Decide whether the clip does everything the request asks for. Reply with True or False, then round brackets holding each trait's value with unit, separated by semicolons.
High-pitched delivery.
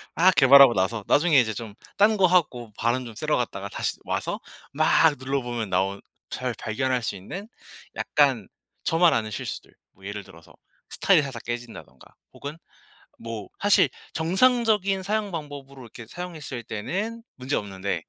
False (130 Hz)